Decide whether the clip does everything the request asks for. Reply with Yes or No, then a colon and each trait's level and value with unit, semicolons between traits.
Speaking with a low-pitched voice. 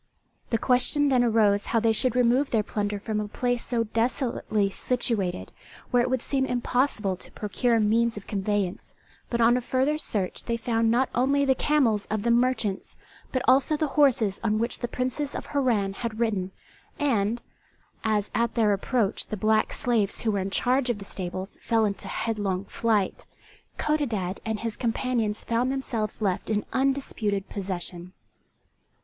No: high, 230 Hz